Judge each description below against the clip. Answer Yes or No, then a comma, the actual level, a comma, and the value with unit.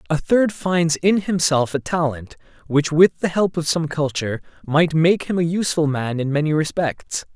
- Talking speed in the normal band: Yes, average, 190 wpm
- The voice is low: No, medium, 160 Hz